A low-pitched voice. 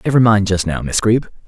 Yes: low, 105 Hz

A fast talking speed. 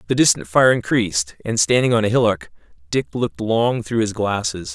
No: average, 190 wpm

